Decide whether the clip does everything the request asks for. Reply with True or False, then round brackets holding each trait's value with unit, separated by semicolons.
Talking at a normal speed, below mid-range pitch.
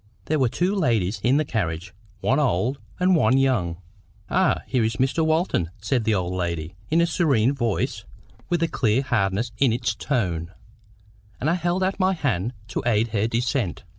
True (180 wpm; 120 Hz)